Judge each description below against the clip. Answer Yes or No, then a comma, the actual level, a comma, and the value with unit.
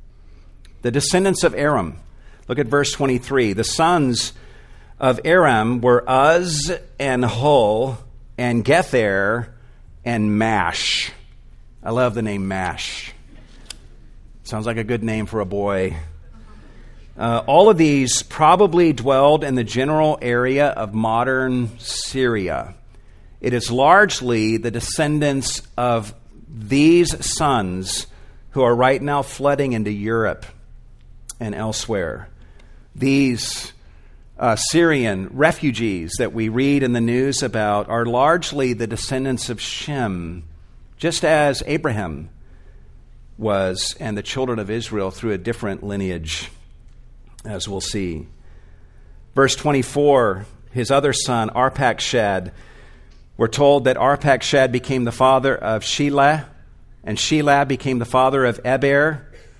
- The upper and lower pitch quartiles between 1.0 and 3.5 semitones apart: No, average, 4.4 semitones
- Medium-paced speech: No, slow, 120 wpm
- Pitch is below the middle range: Yes, low, 120 Hz